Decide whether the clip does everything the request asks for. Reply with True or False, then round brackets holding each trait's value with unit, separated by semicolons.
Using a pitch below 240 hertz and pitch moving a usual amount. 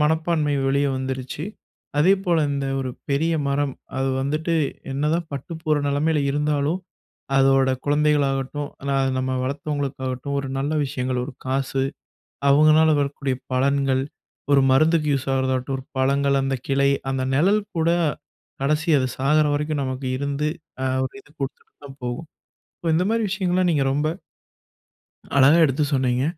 False (140 Hz; 2.3 semitones)